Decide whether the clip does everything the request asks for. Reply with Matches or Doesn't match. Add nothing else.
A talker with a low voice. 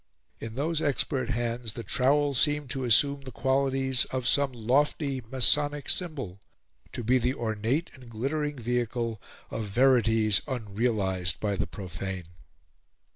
Matches